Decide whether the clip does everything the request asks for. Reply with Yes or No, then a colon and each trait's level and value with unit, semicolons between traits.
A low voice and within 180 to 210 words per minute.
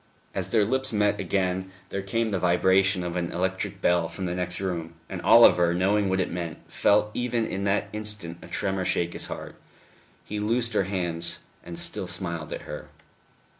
Yes: very low, 95 Hz; average, 185 wpm